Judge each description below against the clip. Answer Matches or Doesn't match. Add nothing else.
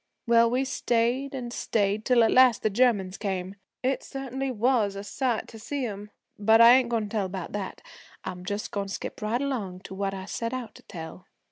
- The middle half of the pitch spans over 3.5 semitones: Matches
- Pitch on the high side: Matches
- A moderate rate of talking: Doesn't match